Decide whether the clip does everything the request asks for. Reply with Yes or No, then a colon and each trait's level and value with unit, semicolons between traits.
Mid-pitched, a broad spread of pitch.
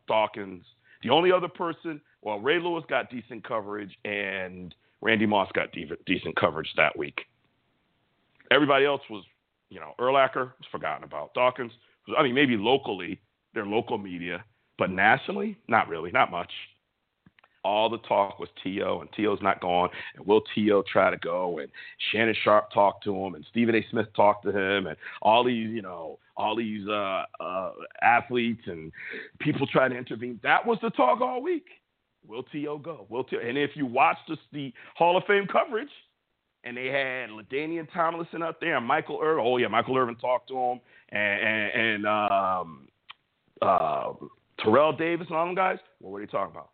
No: low, 125 Hz; wide, 7.1 semitones